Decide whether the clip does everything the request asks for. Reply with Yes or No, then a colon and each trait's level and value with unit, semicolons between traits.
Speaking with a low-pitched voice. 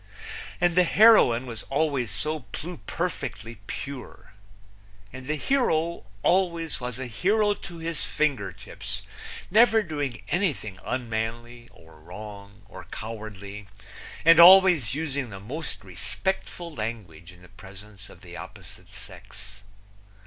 Yes: low, 125 Hz